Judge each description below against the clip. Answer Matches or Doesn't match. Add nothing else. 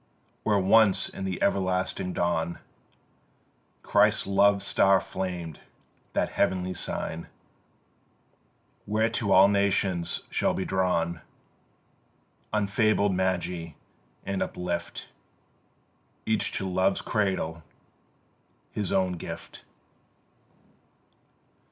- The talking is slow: Matches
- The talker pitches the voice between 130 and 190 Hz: Doesn't match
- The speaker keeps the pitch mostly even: Matches